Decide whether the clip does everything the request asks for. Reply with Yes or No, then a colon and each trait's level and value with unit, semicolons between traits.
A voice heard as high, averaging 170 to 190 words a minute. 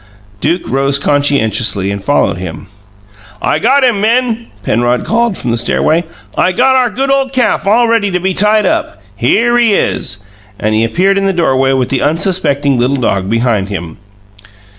No: medium, 150 Hz; average, 175 wpm